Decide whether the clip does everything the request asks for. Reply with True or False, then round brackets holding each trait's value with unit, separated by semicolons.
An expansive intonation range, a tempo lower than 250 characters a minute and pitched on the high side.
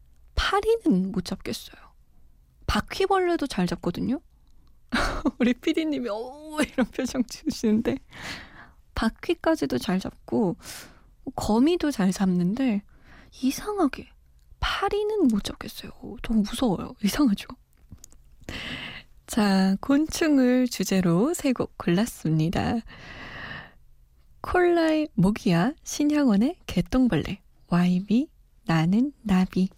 True (7.7 semitones; 210 characters per minute; 240 Hz)